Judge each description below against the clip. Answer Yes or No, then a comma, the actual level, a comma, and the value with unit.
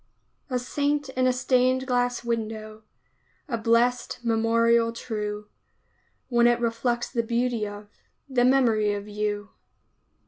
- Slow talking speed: Yes, slow, 125 wpm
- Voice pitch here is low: No, high, 235 Hz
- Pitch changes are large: No, narrow, 2.4 semitones